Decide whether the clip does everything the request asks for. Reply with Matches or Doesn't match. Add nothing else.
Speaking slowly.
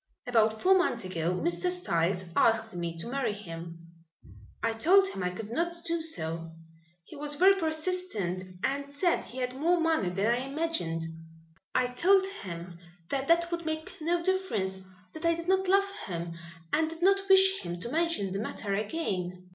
Doesn't match